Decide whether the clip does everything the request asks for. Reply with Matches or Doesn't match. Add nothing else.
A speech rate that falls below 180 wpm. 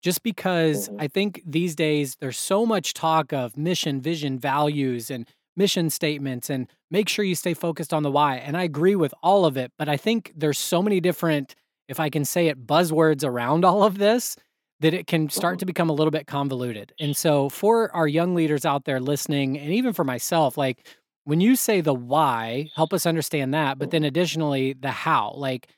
Doesn't match